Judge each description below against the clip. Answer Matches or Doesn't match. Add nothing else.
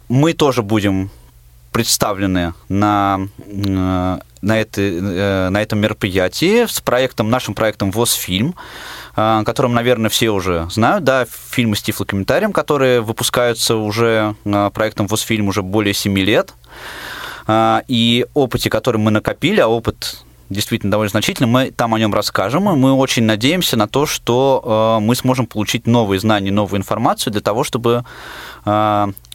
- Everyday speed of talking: Matches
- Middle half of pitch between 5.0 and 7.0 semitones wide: Doesn't match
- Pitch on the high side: Doesn't match